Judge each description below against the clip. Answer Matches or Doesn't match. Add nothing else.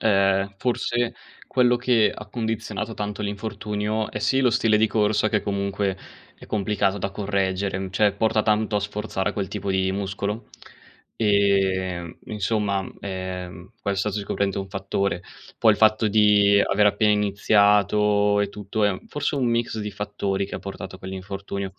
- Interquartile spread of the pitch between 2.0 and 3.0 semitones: Doesn't match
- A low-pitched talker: Matches